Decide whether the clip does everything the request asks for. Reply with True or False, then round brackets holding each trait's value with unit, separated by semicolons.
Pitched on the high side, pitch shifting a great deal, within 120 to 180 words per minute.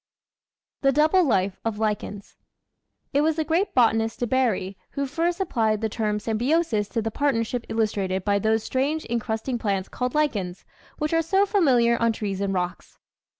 True (230 Hz; 5.7 semitones; 170 wpm)